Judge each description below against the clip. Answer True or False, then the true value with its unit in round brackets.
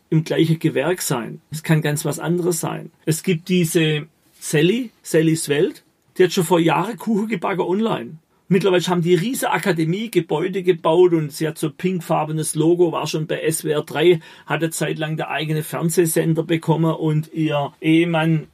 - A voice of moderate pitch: True (165 Hz)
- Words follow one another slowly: False (165 wpm)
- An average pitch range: False (2.3 semitones)